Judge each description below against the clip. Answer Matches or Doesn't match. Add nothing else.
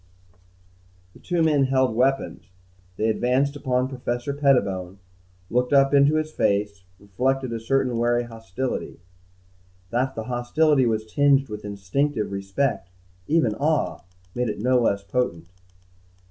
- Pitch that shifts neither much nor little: Matches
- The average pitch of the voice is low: Matches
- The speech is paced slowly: Matches